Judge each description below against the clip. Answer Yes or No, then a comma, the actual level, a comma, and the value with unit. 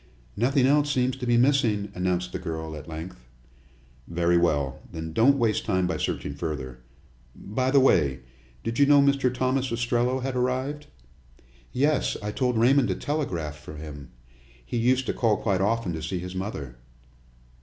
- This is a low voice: Yes, low, 110 Hz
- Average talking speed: Yes, average, 165 wpm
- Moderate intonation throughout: No, wide, 7.8 semitones